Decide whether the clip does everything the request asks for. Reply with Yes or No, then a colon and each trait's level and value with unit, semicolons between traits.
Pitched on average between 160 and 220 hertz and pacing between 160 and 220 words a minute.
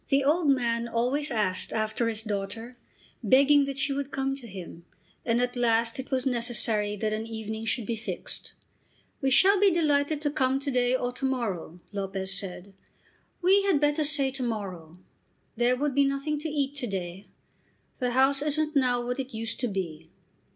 No: high, 245 Hz; average, 185 wpm